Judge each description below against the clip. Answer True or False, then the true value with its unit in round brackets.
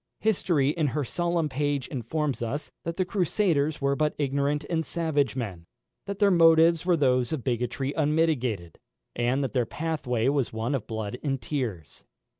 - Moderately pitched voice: True (145 Hz)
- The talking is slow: False (165 wpm)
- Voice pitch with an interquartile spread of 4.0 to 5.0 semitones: True (4.6 semitones)